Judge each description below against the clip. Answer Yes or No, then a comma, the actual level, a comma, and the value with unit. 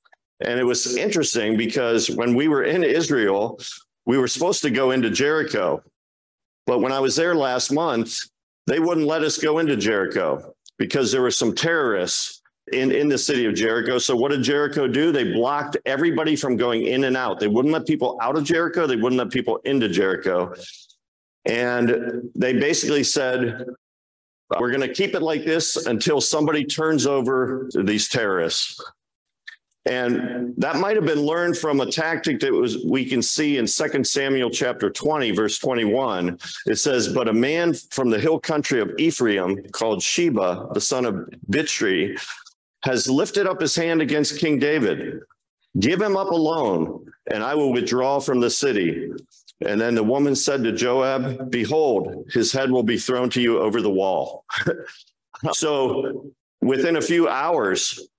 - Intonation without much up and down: No, average, 4.4 semitones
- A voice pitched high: No, low, 135 Hz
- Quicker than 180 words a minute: No, average, 170 wpm